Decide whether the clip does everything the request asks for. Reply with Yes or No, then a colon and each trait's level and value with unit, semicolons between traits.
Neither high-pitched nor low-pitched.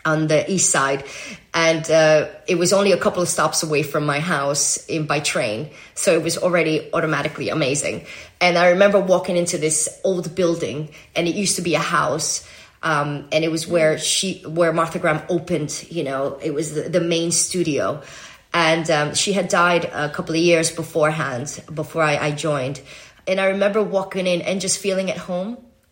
Yes: medium, 165 Hz